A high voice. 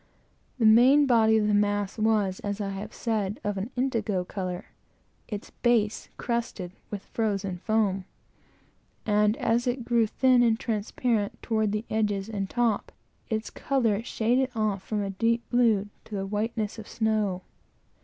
Yes: high, 215 Hz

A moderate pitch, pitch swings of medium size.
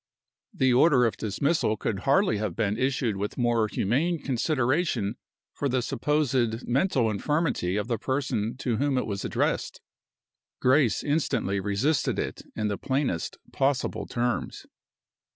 No: low, 125 Hz; average, 4.6 semitones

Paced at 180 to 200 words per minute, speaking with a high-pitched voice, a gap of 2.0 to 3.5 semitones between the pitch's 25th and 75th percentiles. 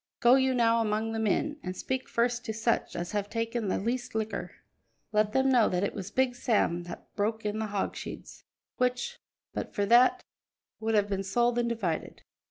Yes: average, 190 wpm; high, 225 Hz; average, 2.8 semitones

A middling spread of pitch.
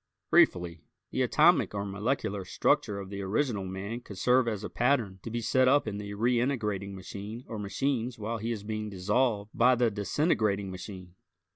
Yes: average, 3.3 semitones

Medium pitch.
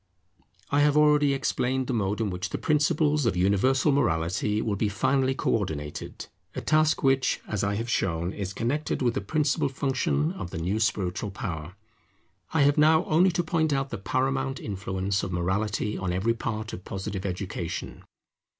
No: low, 115 Hz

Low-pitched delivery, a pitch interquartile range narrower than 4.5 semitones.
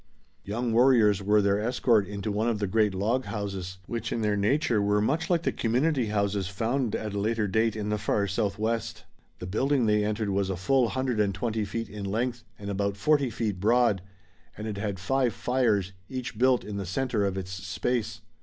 Yes: low, 105 Hz; average, 3.1 semitones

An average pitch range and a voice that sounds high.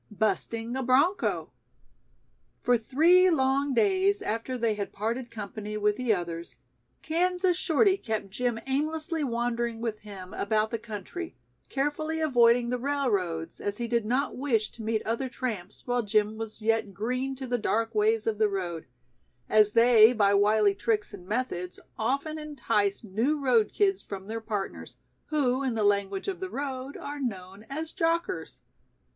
Yes: average, 4.7 semitones; high, 235 Hz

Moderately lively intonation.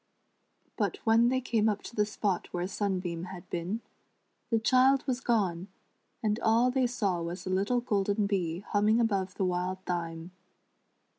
Yes: average, 4.1 semitones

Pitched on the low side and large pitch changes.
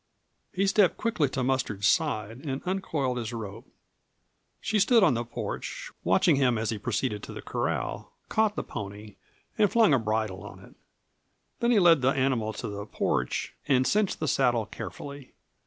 Yes: low, 130 Hz; wide, 8.0 semitones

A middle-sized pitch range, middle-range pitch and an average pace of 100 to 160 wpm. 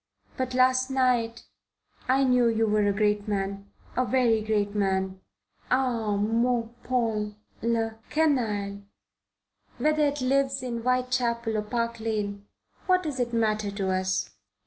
No: average, 3.5 semitones; high, 230 Hz; slow, 135 wpm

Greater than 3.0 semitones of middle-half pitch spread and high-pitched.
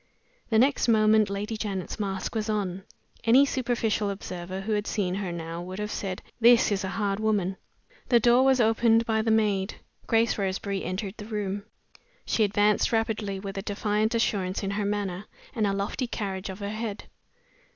No: narrow, 2.4 semitones; high, 210 Hz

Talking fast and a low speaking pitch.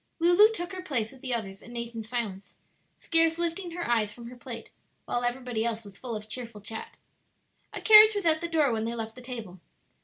No: fast, 220 wpm; high, 245 Hz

